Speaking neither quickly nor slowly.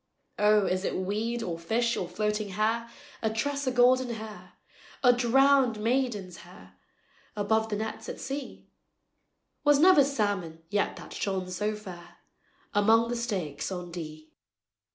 Yes: average, 145 wpm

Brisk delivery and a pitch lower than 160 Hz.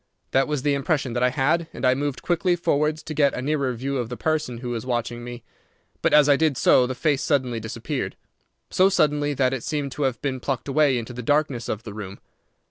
Yes: fast, 230 wpm; low, 135 Hz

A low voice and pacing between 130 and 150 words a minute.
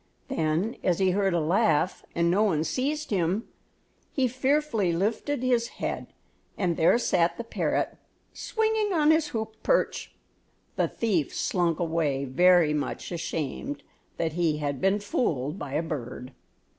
No: medium, 180 Hz; average, 145 wpm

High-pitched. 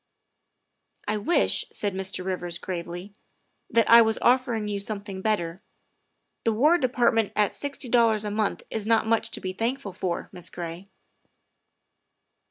Yes: high, 210 Hz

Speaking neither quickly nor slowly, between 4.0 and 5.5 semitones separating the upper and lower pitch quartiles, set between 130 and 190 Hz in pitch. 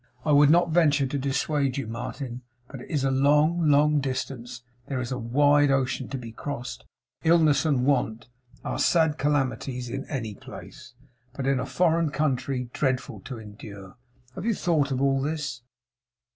No: average, 170 wpm; average, 2.8 semitones; low, 135 Hz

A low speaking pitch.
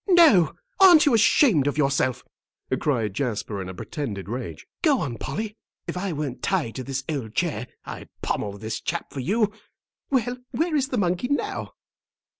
No: medium, 150 Hz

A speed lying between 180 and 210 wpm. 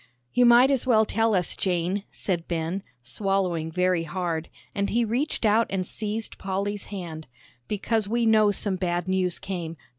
No: average, 160 wpm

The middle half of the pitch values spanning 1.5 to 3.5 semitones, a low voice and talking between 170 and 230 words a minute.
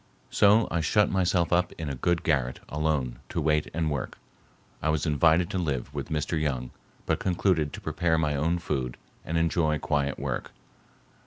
Yes: average, 2.9 semitones; very low, 80 Hz; average, 175 wpm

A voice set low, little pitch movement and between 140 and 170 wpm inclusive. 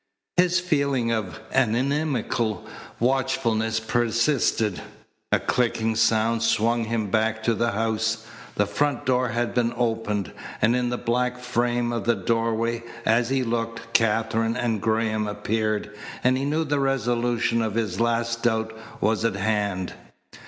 Yes: low, 115 Hz; narrow, 1.7 semitones; average, 145 wpm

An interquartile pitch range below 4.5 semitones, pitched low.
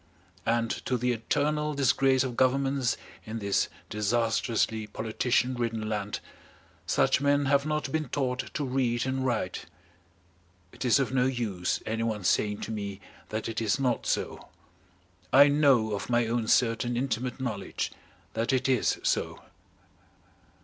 Yes: average, 3.1 semitones; low, 120 Hz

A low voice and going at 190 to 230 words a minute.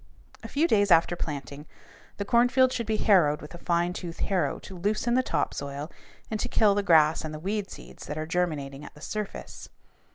No: medium, 175 Hz; fast, 205 wpm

